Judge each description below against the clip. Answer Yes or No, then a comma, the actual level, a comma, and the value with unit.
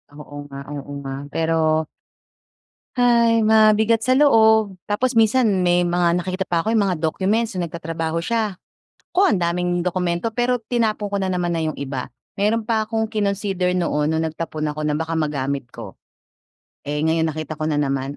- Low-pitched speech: No, medium, 175 Hz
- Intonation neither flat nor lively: No, wide, 5.7 semitones